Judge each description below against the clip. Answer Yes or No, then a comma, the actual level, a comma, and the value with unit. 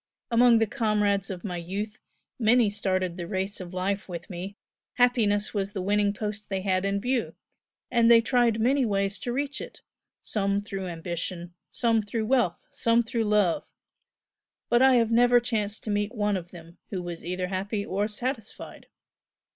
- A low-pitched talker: No, high, 205 Hz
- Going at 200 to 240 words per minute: No, average, 170 wpm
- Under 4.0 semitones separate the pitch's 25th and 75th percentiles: Yes, average, 3.4 semitones